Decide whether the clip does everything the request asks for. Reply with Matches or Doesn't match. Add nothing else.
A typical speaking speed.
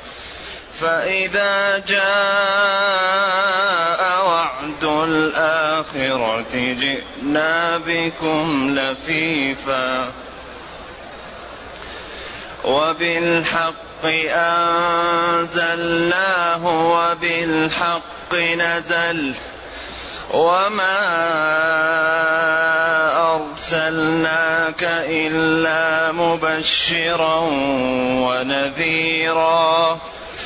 Doesn't match